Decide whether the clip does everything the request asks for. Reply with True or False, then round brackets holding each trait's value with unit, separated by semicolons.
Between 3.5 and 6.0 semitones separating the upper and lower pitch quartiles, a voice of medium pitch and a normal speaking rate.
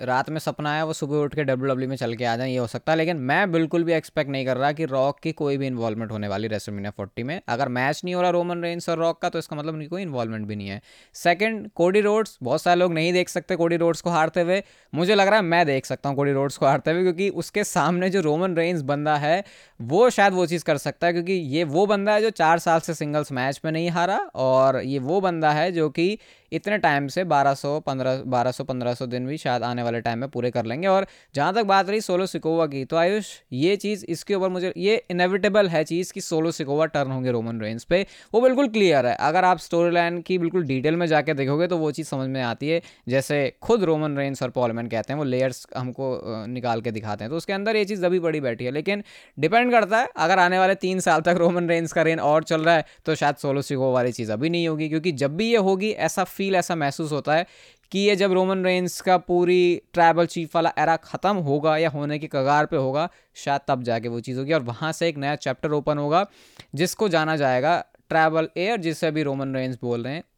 False (4.7 semitones; 160 Hz; 250 wpm)